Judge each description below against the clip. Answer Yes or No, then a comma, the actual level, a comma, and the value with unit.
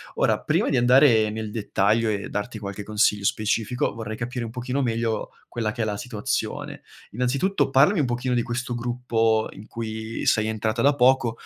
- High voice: No, low, 115 Hz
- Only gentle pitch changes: Yes, narrow, 2.3 semitones